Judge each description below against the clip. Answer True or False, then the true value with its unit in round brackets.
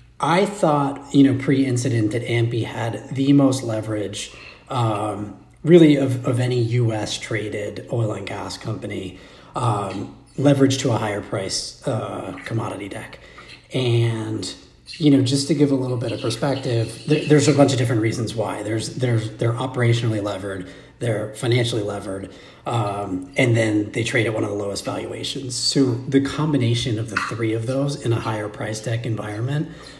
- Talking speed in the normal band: True (170 wpm)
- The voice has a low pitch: True (120 Hz)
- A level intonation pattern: False (4.1 semitones)